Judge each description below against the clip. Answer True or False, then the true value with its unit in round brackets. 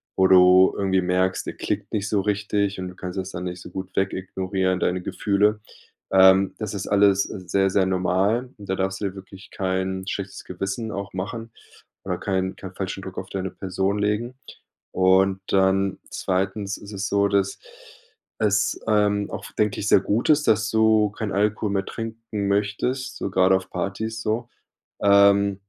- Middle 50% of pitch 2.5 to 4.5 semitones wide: False (1.7 semitones)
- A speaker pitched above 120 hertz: False (100 Hz)